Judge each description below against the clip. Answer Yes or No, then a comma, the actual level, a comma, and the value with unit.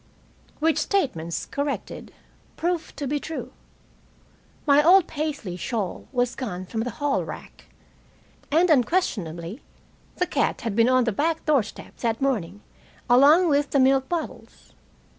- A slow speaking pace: Yes, slow, 130 wpm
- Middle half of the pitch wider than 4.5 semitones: Yes, average, 5.3 semitones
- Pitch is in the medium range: No, very high, 275 Hz